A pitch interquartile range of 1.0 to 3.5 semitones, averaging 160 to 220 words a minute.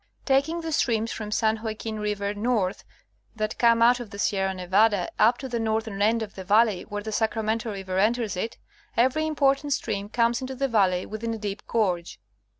Yes: narrow, 2.5 semitones; average, 190 wpm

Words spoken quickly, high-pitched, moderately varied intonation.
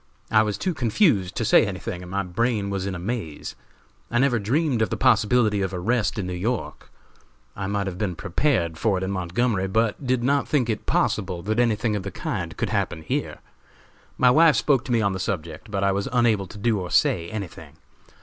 No: fast, 215 wpm; low, 105 Hz; average, 4.1 semitones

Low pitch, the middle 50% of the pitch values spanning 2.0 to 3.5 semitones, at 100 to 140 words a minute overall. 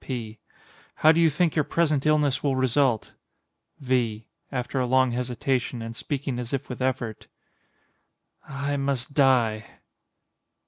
Yes: low, 130 Hz; average, 2.7 semitones; slow, 135 wpm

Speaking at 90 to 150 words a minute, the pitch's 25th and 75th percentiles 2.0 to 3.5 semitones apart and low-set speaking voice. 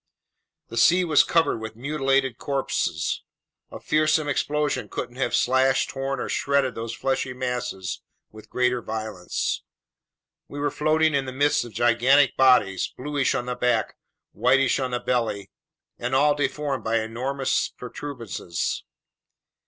Yes: slow, 135 wpm; average, 3.1 semitones; low, 130 Hz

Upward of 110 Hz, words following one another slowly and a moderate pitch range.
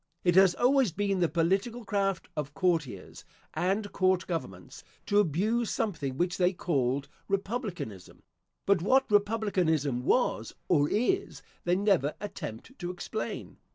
Yes: medium, 185 Hz; slow, 130 wpm; average, 4.5 semitones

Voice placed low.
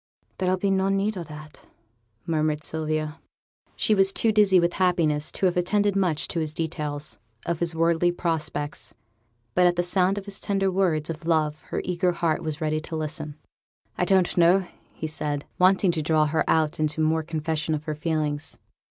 No: medium, 165 Hz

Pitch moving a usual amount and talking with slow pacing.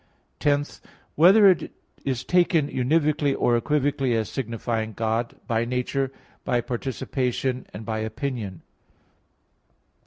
Yes: average, 3.9 semitones; slow, 105 wpm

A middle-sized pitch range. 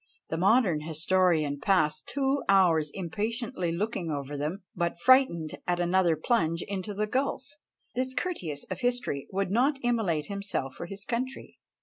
No: wide, 6.2 semitones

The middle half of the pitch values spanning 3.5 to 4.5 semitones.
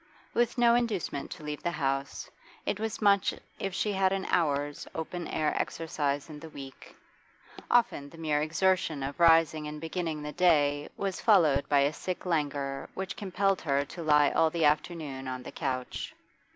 Yes: average, 4.2 semitones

